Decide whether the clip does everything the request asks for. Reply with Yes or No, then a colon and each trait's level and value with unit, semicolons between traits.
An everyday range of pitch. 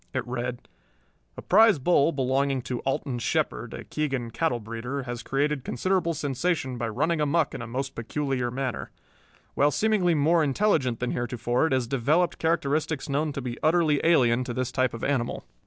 Yes: average, 4.1 semitones